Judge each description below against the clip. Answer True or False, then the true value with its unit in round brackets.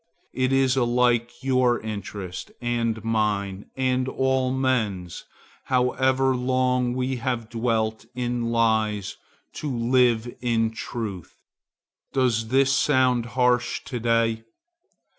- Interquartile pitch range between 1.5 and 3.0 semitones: True (2.4 semitones)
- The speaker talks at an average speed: False (105 wpm)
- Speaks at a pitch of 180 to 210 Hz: False (120 Hz)